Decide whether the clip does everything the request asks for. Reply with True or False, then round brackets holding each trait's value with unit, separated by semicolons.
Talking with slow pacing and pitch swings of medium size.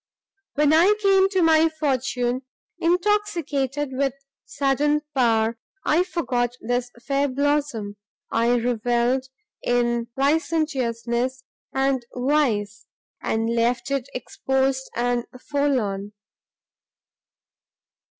True (90 wpm; 3.7 semitones)